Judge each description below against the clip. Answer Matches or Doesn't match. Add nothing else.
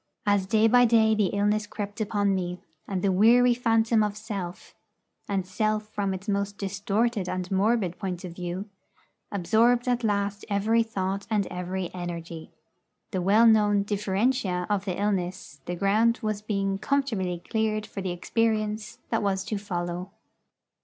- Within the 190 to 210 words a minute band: Doesn't match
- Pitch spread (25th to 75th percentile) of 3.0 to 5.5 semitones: Doesn't match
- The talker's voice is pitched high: Matches